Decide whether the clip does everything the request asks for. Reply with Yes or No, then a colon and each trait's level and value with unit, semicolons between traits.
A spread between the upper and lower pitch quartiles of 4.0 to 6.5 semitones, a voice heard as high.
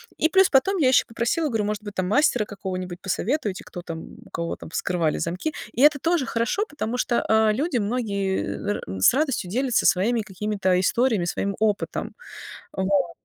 Yes: wide, 5.5 semitones; high, 215 Hz